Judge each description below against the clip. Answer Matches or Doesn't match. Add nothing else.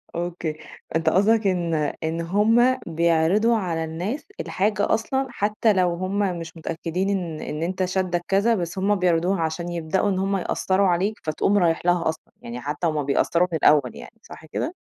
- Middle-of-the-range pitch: Matches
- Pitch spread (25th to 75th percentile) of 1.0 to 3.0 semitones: Doesn't match